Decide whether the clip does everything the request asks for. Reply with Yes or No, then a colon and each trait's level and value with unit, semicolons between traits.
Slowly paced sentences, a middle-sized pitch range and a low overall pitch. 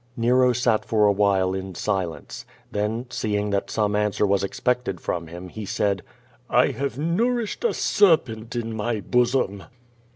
No: average, 155 wpm; average, 3.9 semitones; low, 105 Hz